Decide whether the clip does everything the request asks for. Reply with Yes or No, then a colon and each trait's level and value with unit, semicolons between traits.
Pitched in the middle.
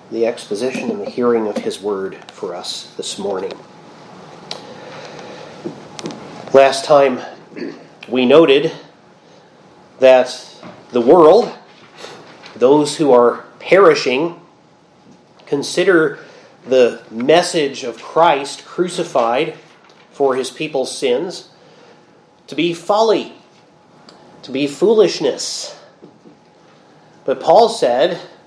Yes: medium, 145 Hz